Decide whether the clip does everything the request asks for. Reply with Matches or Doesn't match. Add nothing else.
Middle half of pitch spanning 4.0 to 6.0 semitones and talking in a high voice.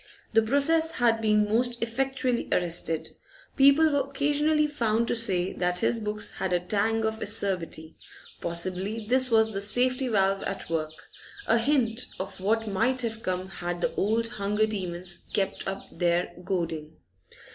Matches